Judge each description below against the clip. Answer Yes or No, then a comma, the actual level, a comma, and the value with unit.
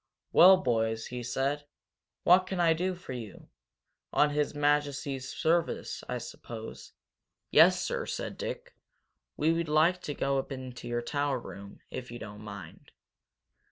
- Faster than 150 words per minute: No, average, 145 wpm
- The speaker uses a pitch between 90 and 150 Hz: Yes, medium, 140 Hz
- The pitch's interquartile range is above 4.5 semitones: Yes, average, 5.1 semitones